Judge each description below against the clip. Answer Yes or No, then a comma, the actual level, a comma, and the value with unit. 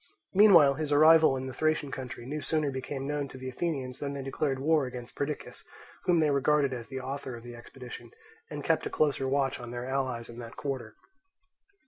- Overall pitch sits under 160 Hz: Yes, low, 135 Hz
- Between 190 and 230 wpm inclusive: Yes, average, 200 wpm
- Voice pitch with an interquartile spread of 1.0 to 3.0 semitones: Yes, average, 2.7 semitones